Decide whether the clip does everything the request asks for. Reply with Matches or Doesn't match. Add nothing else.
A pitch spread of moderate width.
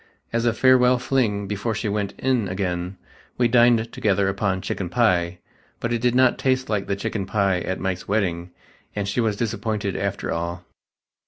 Matches